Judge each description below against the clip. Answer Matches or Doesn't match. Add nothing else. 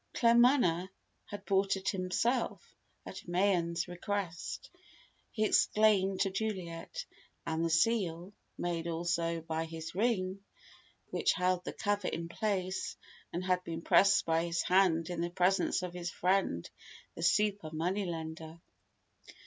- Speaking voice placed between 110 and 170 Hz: Doesn't match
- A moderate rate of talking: Doesn't match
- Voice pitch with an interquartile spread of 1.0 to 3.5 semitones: Matches